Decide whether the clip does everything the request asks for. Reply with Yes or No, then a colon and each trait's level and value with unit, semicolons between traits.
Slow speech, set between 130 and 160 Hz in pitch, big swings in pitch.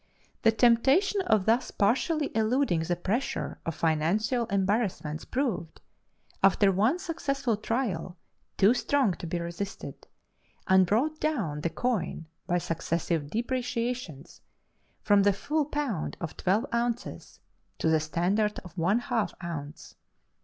No: slow, 125 wpm; high, 210 Hz; wide, 6.3 semitones